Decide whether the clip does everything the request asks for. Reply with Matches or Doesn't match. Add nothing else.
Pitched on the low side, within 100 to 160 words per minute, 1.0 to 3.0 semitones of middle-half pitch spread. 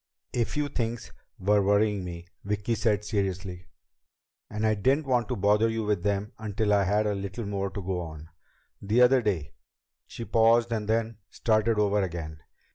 Doesn't match